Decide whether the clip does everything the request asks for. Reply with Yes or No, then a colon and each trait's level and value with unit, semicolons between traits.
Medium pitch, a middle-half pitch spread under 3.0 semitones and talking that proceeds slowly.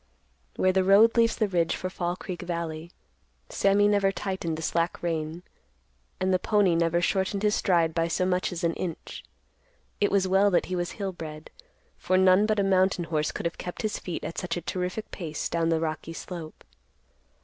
No: medium, 180 Hz; narrow, 2.6 semitones; average, 195 wpm